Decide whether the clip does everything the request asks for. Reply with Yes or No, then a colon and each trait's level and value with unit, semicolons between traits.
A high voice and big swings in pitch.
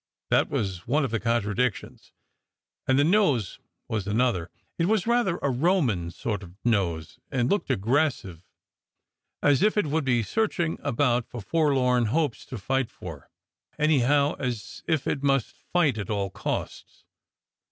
No: low, 125 Hz; wide, 6.3 semitones